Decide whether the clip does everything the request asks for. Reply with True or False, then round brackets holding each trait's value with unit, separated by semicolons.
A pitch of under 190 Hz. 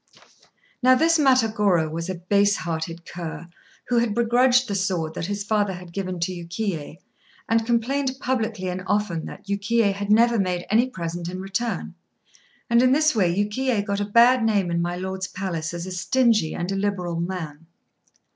False (200 Hz)